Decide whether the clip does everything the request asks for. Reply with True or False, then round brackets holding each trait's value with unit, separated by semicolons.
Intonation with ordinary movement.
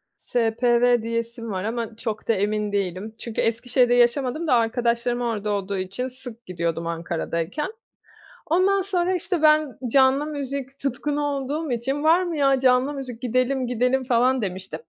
True (3.7 semitones)